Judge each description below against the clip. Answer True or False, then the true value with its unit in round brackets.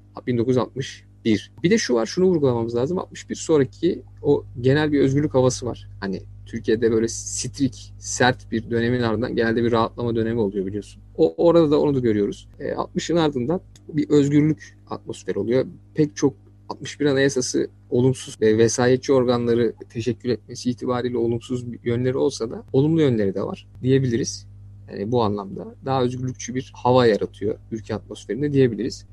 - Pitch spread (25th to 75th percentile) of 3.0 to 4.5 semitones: True (4.1 semitones)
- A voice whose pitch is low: True (120 Hz)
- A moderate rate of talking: False (155 wpm)